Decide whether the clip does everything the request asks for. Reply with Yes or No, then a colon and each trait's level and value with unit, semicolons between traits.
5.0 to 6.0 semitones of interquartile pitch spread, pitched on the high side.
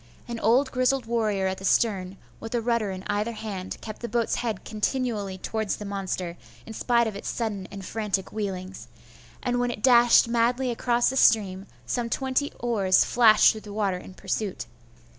No: average, 3.5 semitones; high, 220 Hz